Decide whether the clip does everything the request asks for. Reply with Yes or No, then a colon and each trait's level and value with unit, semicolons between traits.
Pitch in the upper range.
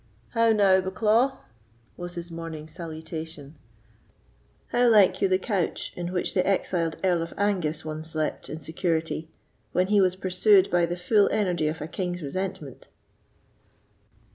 No: medium, 175 Hz